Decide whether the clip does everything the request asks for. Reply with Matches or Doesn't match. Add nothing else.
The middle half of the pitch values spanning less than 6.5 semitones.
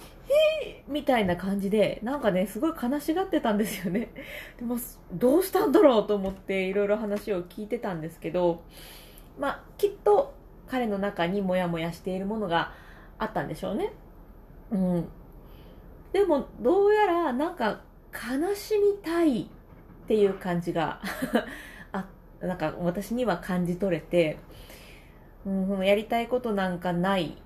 Doesn't match